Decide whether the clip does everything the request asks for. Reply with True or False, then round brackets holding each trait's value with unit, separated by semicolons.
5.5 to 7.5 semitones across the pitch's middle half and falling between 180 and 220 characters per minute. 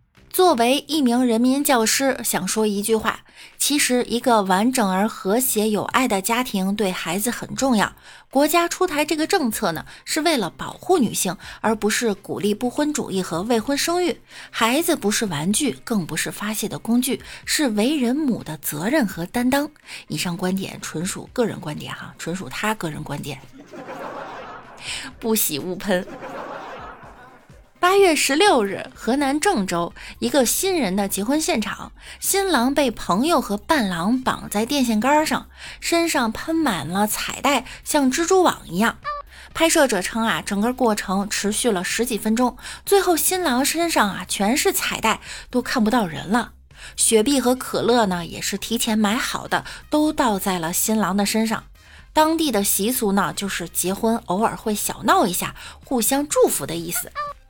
False (6.2 semitones; 245 characters per minute)